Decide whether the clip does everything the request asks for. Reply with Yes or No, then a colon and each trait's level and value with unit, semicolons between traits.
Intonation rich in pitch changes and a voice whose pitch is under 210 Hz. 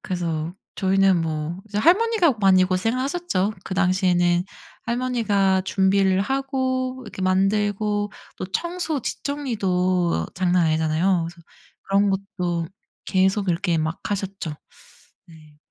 No: average, 3.3 semitones; high, 190 Hz